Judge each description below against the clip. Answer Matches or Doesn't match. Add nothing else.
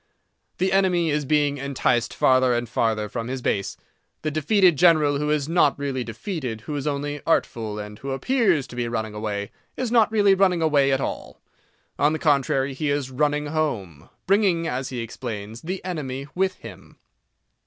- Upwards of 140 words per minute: Matches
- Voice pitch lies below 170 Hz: Matches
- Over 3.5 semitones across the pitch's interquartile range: Matches